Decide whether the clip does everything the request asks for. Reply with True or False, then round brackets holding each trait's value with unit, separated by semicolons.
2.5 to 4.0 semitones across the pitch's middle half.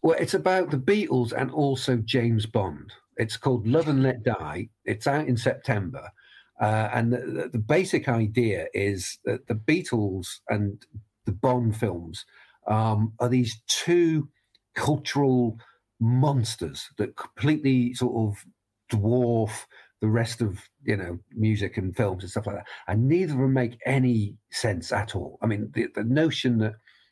True (3.6 semitones)